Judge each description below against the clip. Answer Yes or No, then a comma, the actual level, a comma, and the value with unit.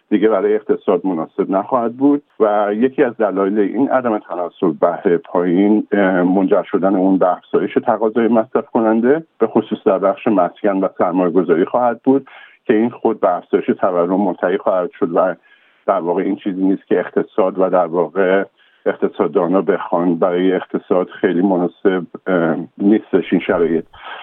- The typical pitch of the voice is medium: No, low, 110 Hz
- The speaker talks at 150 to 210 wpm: Yes, fast, 155 wpm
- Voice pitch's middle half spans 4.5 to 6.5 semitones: Yes, average, 4.9 semitones